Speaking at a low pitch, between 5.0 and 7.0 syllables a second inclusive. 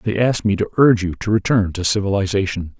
Yes: low, 100 Hz; 6.6 syllables/s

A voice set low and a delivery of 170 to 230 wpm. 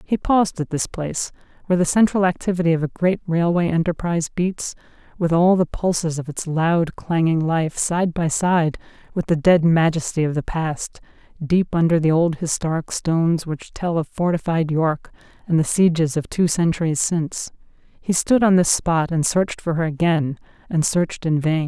No: medium, 165 Hz; average, 175 wpm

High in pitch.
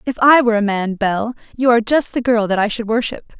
Yes: high, 230 Hz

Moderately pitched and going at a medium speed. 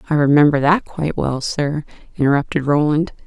Yes: medium, 150 Hz; average, 145 wpm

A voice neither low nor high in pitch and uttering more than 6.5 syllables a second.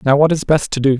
Yes: medium, 145 Hz; 6.9 syllables/s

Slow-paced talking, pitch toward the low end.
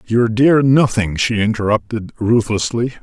Yes: slow, 120 wpm; low, 115 Hz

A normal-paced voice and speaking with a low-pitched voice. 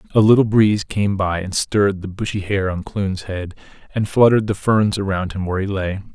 No: fast, 215 wpm; low, 100 Hz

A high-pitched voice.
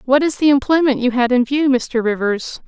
Yes: very high, 260 Hz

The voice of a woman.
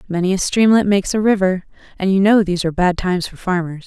Yes: female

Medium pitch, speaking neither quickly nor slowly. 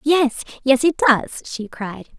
No: very high, 260 Hz; average, 165 wpm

